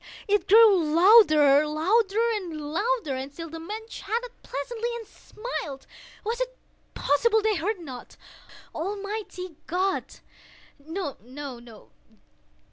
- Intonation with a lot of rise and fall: Yes, wide, 6.6 semitones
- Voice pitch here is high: Yes, very high, 370 Hz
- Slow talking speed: Yes, slow, 95 wpm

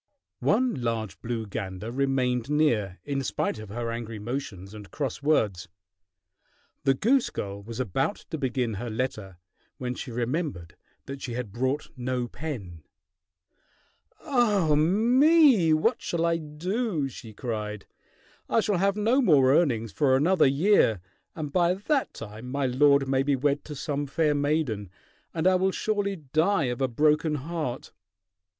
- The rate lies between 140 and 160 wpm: Yes, average, 150 wpm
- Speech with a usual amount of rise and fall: No, wide, 6.0 semitones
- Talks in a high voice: No, low, 135 Hz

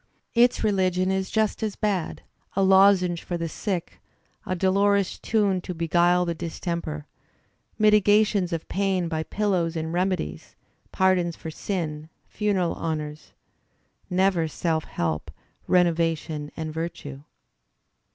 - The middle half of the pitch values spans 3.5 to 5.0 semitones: No, average, 3.1 semitones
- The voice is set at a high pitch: No, medium, 180 Hz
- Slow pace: Yes, slow, 120 wpm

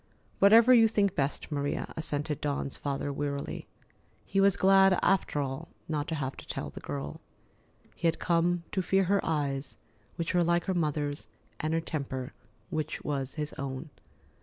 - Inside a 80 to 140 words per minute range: No, average, 165 wpm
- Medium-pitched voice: Yes, medium, 155 Hz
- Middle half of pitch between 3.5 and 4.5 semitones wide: Yes, average, 4.1 semitones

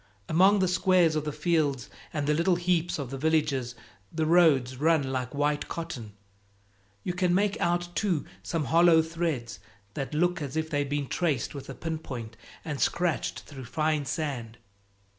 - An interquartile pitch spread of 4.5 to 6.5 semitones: No, average, 3.8 semitones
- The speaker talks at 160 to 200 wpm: Yes, average, 170 wpm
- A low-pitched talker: No, medium, 155 Hz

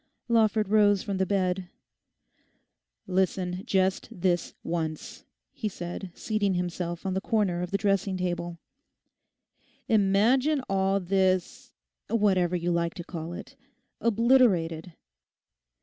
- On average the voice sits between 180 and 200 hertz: Yes, high, 190 Hz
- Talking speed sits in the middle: No, slow, 105 wpm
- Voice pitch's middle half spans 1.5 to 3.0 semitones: Yes, average, 2.7 semitones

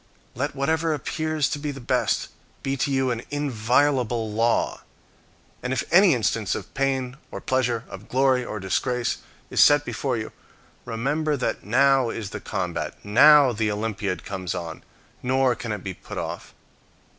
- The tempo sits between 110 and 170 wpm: Yes, average, 160 wpm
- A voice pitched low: Yes, low, 125 Hz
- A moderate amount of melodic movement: Yes, average, 3.8 semitones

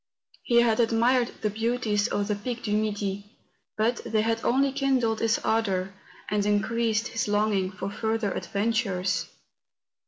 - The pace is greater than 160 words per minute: No, average, 145 wpm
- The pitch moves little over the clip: Yes, narrow, 2.1 semitones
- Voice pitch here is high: Yes, high, 220 Hz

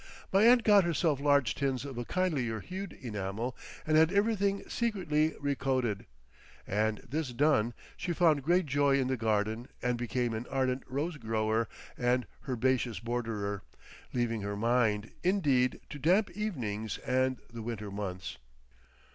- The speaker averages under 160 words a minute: Yes, average, 145 wpm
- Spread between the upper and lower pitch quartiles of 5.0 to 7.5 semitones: Yes, wide, 5.6 semitones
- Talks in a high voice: No, low, 130 Hz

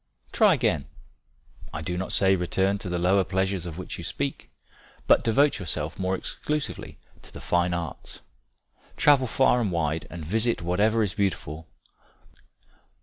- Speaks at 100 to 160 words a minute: Yes, average, 150 wpm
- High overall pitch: No, very low, 95 Hz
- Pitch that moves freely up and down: No, average, 3.6 semitones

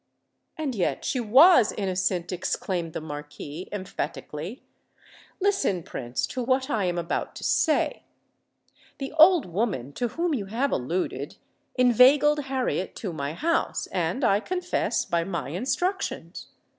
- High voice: Yes, high, 210 Hz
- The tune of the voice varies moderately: No, wide, 7.8 semitones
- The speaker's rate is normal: No, slow, 130 wpm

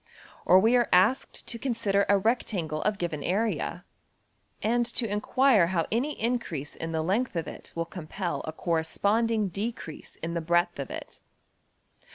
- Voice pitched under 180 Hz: No, high, 195 Hz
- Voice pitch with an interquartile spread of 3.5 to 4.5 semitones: No, wide, 5.5 semitones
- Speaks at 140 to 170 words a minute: Yes, average, 160 wpm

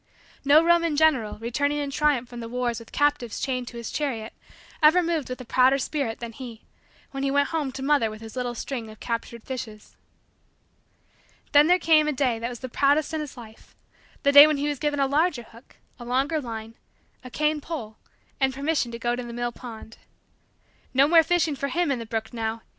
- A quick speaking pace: Yes, fast, 210 wpm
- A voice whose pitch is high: Yes, very high, 265 Hz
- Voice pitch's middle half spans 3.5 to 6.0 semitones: Yes, average, 4.0 semitones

